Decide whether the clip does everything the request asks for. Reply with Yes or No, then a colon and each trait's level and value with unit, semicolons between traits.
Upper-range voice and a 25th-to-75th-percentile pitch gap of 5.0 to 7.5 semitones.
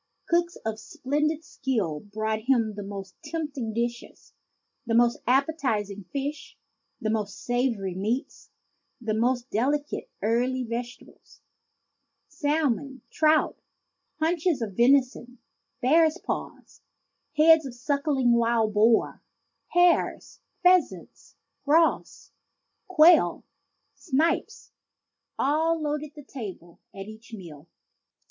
Yes: very high, 255 Hz; wide, 5.5 semitones